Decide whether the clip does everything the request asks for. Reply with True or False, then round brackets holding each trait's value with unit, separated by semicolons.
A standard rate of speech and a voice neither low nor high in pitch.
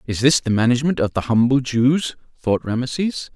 False (180 wpm; 125 Hz)